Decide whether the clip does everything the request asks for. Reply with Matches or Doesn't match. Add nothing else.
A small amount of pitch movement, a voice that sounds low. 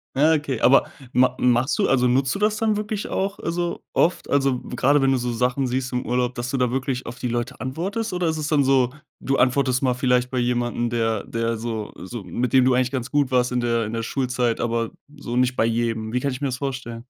Matches